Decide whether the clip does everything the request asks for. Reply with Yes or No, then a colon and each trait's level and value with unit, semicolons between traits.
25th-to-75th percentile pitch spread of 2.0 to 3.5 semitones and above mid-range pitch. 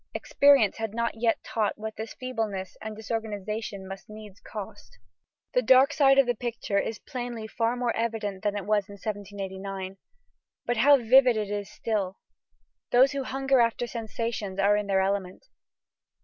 Yes: average, 3.1 semitones; high, 220 Hz